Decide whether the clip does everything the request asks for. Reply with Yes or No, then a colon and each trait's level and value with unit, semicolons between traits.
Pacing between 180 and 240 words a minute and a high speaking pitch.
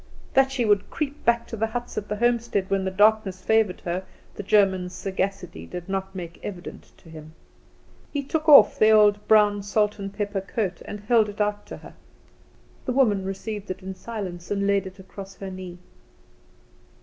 Yes: average, 185 wpm; high, 200 Hz